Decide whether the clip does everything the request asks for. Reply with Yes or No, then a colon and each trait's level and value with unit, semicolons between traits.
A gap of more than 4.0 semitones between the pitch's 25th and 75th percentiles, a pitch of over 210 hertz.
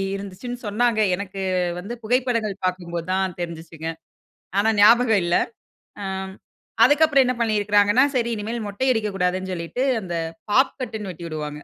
No: average, 4.4 semitones; high, 205 Hz